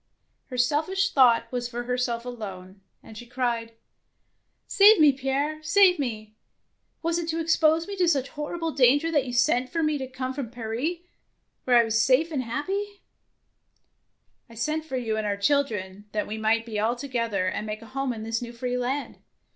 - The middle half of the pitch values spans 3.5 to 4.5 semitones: No, average, 5.1 semitones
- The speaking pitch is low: No, very high, 255 Hz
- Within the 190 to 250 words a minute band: Yes, average, 195 wpm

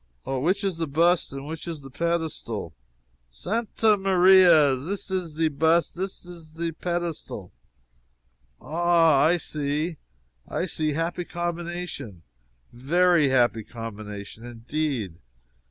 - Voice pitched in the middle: Yes, medium, 160 Hz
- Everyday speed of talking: No, slow, 110 wpm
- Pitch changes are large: No, average, 4.3 semitones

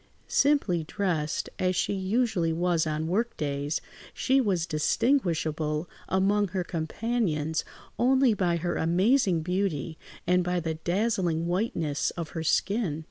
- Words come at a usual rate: No, slow, 130 wpm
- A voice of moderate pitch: Yes, medium, 175 Hz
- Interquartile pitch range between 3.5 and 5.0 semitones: Yes, average, 4.2 semitones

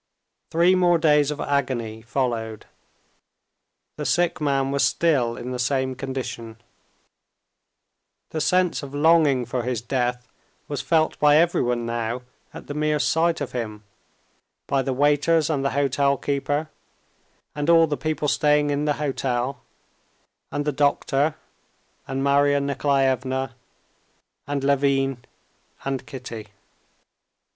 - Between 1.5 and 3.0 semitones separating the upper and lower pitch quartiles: Yes, average, 2.7 semitones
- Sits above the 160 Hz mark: No, medium, 140 Hz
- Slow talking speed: Yes, slow, 125 wpm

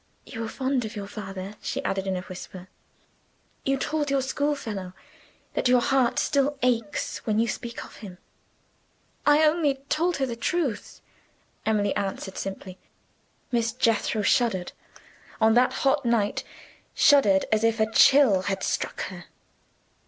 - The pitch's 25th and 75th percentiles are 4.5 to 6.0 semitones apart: Yes, average, 5.1 semitones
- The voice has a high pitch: Yes, high, 230 Hz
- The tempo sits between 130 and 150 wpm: Yes, average, 145 wpm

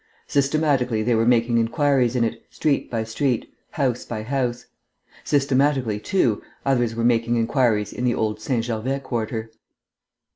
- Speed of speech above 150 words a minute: No, average, 145 wpm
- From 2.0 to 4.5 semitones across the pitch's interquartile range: Yes, average, 3.1 semitones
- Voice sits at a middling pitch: No, low, 120 Hz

